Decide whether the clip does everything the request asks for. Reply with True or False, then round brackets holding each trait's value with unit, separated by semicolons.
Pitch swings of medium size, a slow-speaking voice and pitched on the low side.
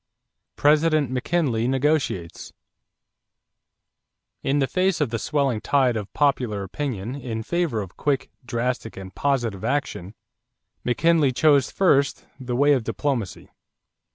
True (4.3 semitones; 120 wpm; 130 Hz)